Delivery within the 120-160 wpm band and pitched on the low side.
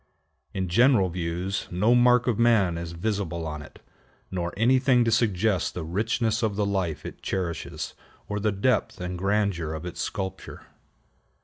Yes: average, 155 wpm; very low, 95 Hz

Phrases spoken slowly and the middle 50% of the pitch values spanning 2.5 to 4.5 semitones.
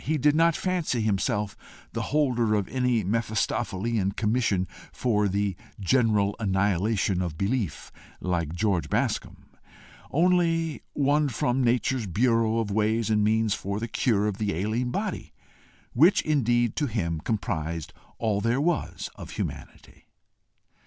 Yes: slow, 130 wpm; average, 3.9 semitones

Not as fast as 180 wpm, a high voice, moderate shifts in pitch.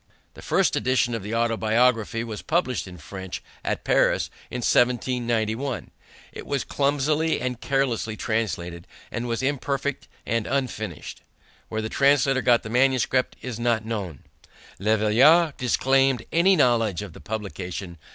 No: average, 140 wpm; low, 120 Hz; average, 3.5 semitones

